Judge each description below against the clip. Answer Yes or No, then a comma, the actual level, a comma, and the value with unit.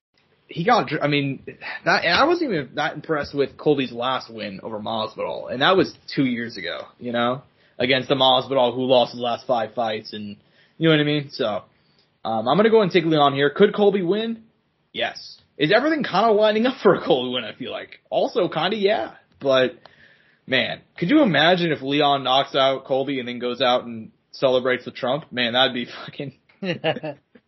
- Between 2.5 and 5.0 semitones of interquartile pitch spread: Yes, average, 4.3 semitones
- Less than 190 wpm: No, fast, 205 wpm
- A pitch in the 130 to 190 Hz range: Yes, low, 135 Hz